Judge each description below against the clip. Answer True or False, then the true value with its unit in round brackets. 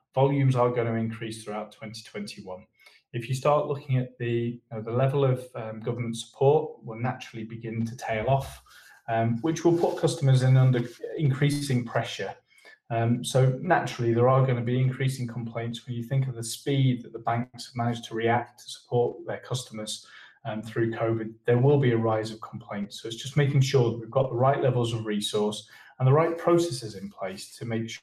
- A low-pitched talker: True (120 Hz)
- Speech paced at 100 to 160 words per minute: False (205 wpm)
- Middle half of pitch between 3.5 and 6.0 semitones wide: False (2.6 semitones)